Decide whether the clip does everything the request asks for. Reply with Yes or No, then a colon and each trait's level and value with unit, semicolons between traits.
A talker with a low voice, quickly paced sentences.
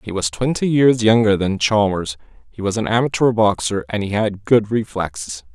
No: low, 110 Hz; average, 185 wpm